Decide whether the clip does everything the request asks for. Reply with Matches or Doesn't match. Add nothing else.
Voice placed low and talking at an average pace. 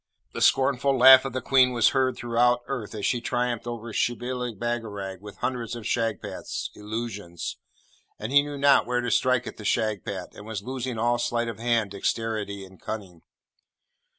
Matches